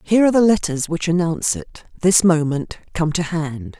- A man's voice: No, female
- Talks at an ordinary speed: Yes, average, 190 wpm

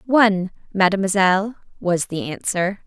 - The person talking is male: No, female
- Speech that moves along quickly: No, slow, 105 wpm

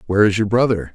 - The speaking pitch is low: Yes, low, 105 Hz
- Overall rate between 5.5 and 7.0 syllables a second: No, 7.6 syllables/s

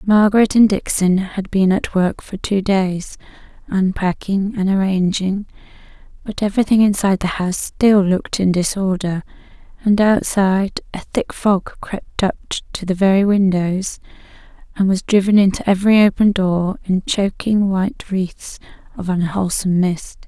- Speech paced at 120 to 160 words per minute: Yes, average, 140 wpm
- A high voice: Yes, high, 195 Hz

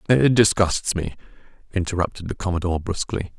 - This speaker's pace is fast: No, slow, 125 wpm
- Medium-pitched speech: No, very low, 95 Hz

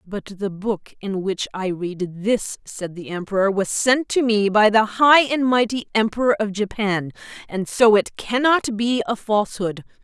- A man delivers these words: No, female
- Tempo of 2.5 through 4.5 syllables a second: Yes, 4.3 syllables/s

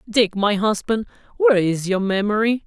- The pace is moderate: Yes, average, 155 wpm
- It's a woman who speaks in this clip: No, male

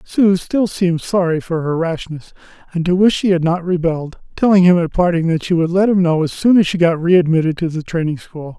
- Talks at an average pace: No, fast, 245 wpm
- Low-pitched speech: No, medium, 170 Hz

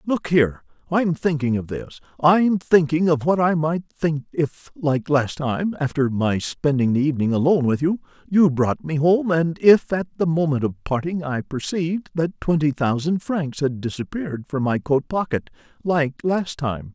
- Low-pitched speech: No, medium, 155 Hz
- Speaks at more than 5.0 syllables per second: No, 4.6 syllables/s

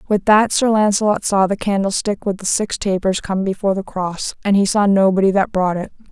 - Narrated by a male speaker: No, female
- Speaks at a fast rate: Yes, fast, 215 wpm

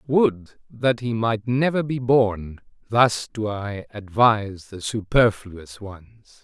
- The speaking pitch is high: No, low, 110 Hz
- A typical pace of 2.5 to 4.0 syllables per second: Yes, 3.2 syllables/s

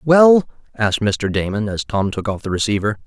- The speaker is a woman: No, male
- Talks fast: No, average, 195 wpm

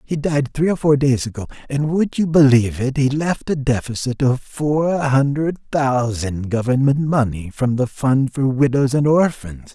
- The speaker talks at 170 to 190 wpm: Yes, average, 180 wpm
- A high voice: No, low, 135 Hz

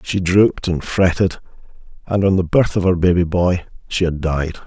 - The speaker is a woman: No, male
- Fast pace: No, average, 195 wpm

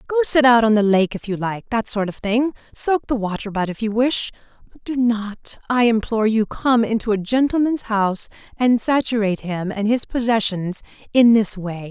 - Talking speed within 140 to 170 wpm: No, average, 200 wpm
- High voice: Yes, high, 225 Hz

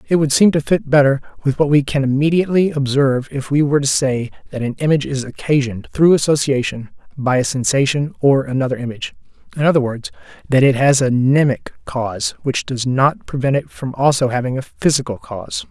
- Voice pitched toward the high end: No, low, 135 Hz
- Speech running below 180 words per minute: No, average, 185 wpm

